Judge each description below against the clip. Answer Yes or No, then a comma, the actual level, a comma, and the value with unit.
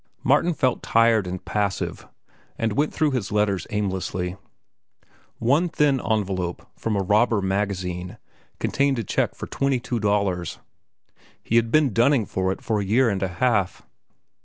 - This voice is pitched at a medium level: No, low, 105 Hz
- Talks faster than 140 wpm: Yes, average, 155 wpm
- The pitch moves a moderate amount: Yes, average, 4.6 semitones